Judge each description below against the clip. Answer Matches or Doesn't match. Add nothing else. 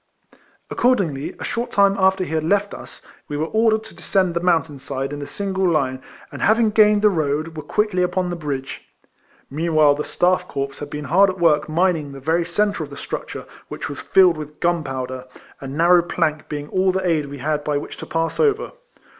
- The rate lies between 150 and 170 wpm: Doesn't match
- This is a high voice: Doesn't match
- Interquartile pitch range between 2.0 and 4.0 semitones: Doesn't match